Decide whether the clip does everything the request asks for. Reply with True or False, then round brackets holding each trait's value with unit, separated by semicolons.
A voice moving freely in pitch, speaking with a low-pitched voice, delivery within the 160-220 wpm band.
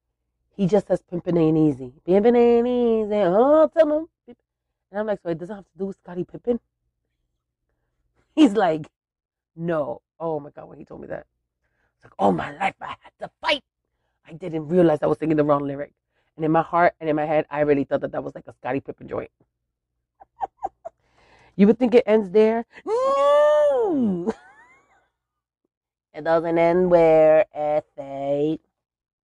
False (7.0 semitones; 165 Hz; 170 wpm)